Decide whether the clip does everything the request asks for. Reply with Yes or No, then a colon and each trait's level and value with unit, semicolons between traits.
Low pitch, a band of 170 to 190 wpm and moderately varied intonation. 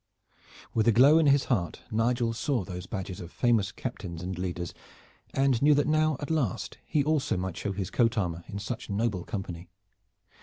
No: low, 110 Hz; average, 185 wpm; wide, 6.6 semitones